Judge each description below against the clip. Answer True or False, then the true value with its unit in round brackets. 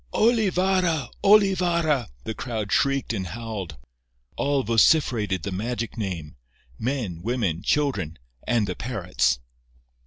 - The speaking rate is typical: False (100 wpm)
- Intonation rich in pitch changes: True (7.6 semitones)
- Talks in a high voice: False (115 Hz)